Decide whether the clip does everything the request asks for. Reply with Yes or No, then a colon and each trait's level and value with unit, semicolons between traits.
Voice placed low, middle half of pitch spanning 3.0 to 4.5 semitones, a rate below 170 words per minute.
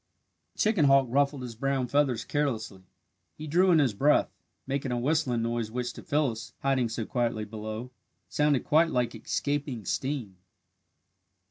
Yes: low, 130 Hz; average, 3.9 semitones; average, 150 wpm